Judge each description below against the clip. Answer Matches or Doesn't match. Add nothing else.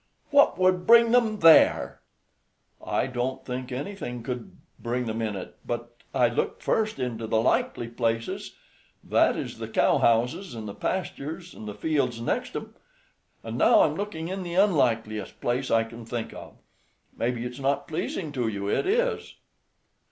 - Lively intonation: Matches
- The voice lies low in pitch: Matches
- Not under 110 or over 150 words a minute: Doesn't match